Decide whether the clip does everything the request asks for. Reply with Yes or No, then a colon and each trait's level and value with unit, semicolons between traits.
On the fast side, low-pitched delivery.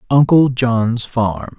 No: slow, 115 wpm; low, 120 Hz